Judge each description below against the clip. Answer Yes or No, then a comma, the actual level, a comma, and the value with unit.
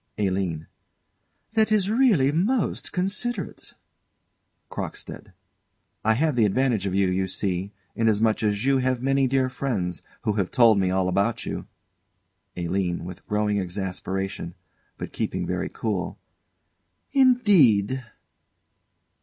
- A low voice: Yes, low, 110 Hz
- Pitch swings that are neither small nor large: No, wide, 6.3 semitones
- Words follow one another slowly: Yes, slow, 120 wpm